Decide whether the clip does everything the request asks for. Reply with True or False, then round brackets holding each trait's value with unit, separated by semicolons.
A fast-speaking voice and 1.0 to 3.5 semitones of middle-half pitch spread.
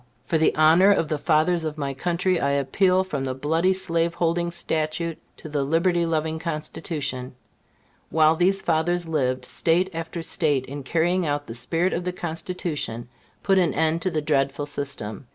False (170 wpm; 3.1 semitones)